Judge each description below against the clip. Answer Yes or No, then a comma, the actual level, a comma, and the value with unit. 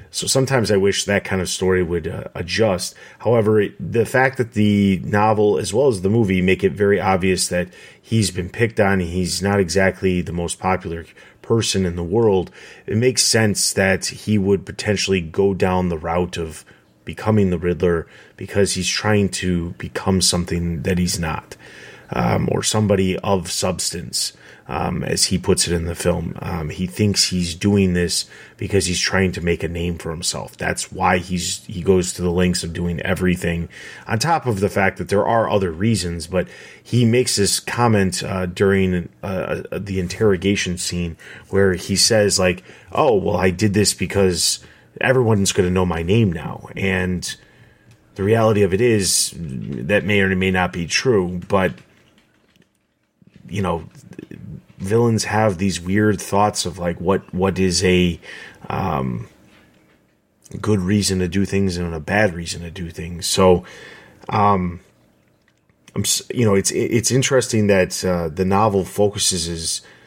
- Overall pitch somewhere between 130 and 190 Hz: No, very low, 95 Hz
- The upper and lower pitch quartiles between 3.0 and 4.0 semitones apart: No, narrow, 2.6 semitones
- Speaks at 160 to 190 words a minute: Yes, average, 170 wpm